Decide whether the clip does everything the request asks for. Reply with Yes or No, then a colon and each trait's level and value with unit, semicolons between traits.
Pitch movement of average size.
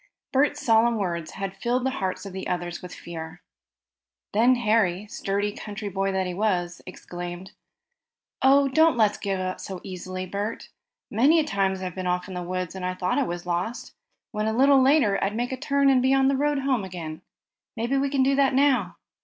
No: wide, 6.1 semitones